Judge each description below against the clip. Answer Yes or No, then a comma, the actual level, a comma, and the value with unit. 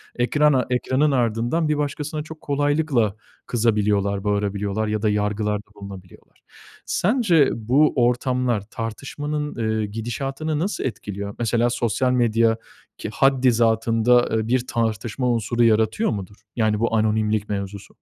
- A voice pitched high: No, low, 115 Hz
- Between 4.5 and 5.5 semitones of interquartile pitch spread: No, average, 4.0 semitones